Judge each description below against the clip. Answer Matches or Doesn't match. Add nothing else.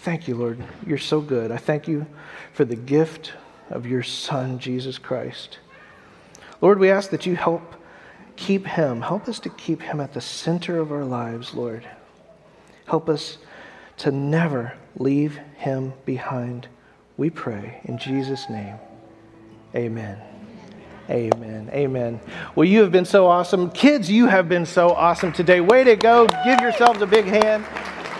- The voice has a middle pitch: Matches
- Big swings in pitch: Matches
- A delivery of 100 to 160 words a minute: Matches